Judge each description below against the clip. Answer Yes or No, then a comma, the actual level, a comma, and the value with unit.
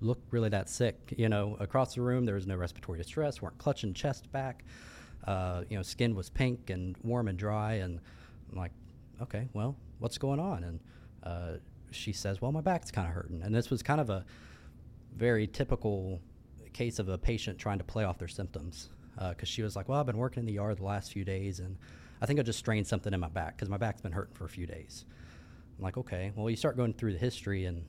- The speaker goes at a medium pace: No, fast, 235 wpm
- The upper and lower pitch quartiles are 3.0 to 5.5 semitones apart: Yes, average, 4.7 semitones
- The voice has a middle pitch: No, low, 105 Hz